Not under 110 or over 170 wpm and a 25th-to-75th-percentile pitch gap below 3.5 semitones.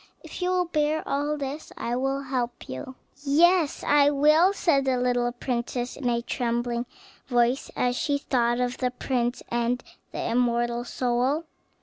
Yes: average, 155 wpm; average, 3.0 semitones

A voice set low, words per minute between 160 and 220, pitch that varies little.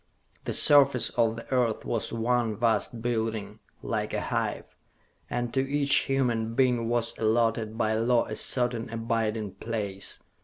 No: low, 115 Hz; average, 145 wpm; narrow, 1.6 semitones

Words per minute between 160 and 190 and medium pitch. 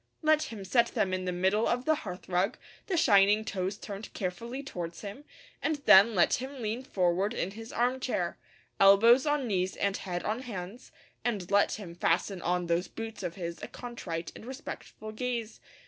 No: average, 180 wpm; high, 205 Hz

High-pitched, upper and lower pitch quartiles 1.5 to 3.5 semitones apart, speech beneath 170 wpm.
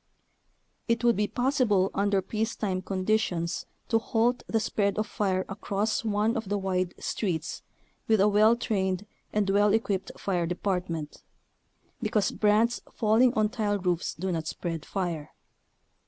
Yes: high, 205 Hz; average, 2.8 semitones; average, 145 wpm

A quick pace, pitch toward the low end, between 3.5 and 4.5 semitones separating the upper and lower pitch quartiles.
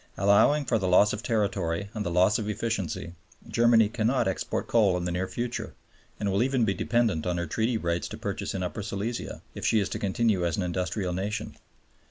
Yes: fast, 210 wpm; low, 100 Hz; average, 3.8 semitones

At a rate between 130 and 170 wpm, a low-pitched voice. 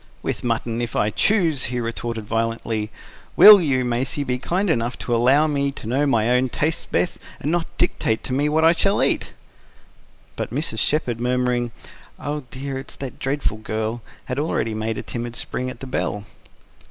No: average, 180 wpm; low, 125 Hz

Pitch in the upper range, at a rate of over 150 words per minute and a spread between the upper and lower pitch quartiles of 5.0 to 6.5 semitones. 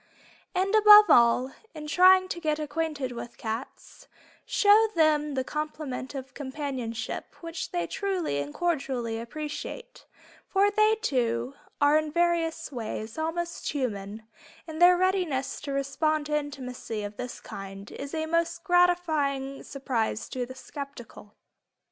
No: very high, 290 Hz; slow, 135 wpm; average, 5.3 semitones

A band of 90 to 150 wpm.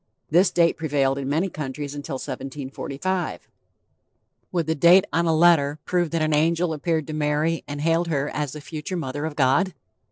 No: average, 180 wpm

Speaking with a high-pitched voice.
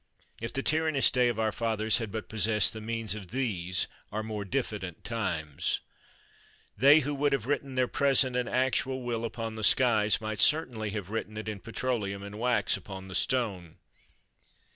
No: low, 110 Hz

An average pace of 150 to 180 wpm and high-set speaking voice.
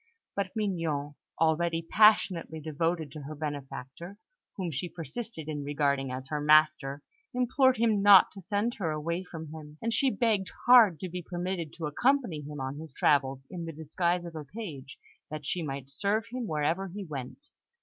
No: average, 175 wpm; medium, 165 Hz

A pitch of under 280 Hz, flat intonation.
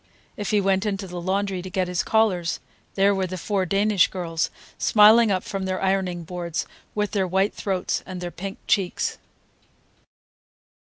Yes: high, 190 Hz; narrow, 1.9 semitones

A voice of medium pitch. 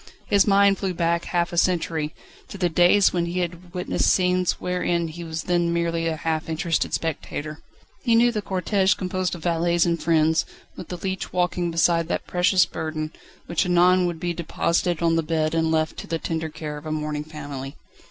Yes: medium, 170 Hz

